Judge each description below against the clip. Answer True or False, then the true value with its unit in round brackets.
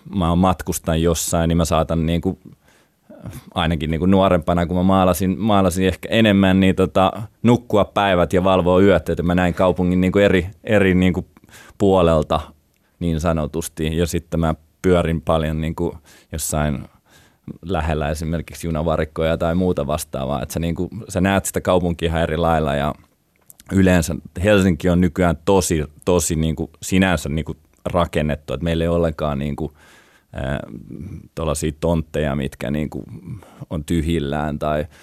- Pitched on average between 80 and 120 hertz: True (85 Hz)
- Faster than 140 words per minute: True (150 wpm)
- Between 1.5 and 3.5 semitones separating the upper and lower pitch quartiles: True (2.7 semitones)